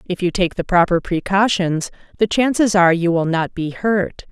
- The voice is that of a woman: Yes, female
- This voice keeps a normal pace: Yes, average, 195 wpm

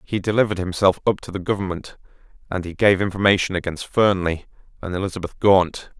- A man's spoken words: Yes, male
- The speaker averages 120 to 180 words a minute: Yes, average, 160 wpm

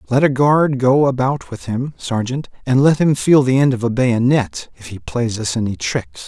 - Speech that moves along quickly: Yes, fast, 220 wpm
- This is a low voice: Yes, low, 130 Hz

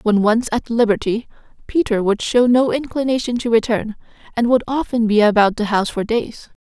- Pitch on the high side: Yes, high, 230 Hz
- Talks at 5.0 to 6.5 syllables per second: Yes, 5.3 syllables/s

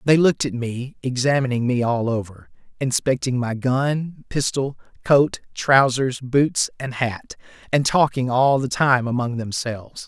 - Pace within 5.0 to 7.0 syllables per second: No, 4.2 syllables/s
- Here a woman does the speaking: No, male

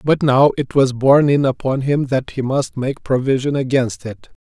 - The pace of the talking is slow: No, fast, 205 wpm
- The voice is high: No, low, 135 Hz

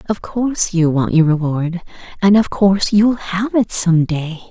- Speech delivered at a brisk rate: No, average, 185 wpm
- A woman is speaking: Yes, female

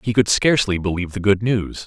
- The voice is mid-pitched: No, low, 105 Hz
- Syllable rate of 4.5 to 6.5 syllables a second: Yes, 6.2 syllables/s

